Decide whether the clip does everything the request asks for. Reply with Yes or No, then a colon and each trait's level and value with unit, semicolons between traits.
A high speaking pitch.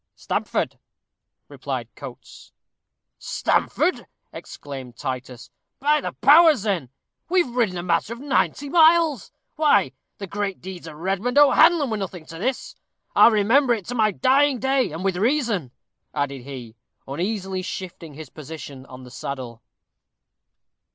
Yes: high, 195 Hz